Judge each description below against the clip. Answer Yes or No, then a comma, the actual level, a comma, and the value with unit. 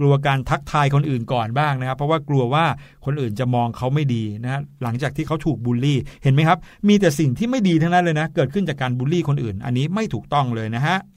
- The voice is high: No, medium, 140 Hz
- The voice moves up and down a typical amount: Yes, average, 4.2 semitones